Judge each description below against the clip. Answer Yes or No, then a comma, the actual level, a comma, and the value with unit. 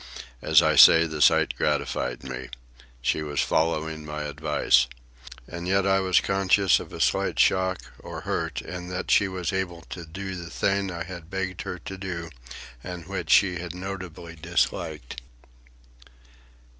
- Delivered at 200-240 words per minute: No, average, 155 wpm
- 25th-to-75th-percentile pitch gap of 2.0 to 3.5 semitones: Yes, average, 3.0 semitones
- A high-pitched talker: No, very low, 90 Hz